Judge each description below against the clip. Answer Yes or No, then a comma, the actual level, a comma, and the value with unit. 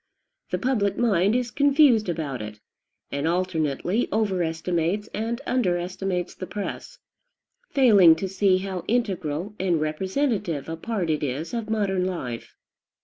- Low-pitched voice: No, medium, 185 Hz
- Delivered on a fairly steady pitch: No, average, 5.0 semitones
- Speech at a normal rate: No, slow, 130 wpm